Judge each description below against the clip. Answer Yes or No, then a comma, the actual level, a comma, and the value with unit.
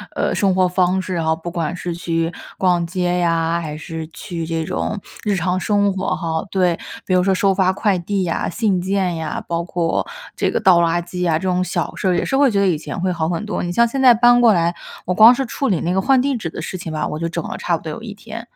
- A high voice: No, medium, 180 Hz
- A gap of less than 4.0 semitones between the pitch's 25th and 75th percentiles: Yes, average, 2.8 semitones